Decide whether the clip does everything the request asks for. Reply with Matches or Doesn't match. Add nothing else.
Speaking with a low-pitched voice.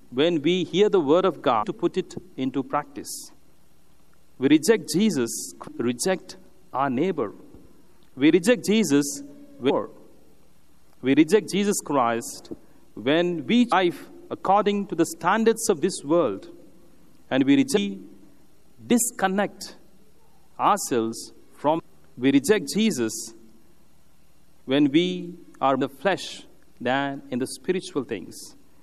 Doesn't match